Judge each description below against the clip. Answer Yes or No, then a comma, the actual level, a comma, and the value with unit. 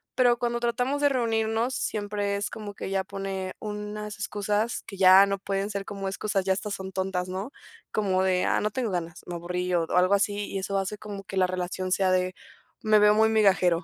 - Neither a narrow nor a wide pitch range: No, narrow, 2.2 semitones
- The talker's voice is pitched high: Yes, high, 200 Hz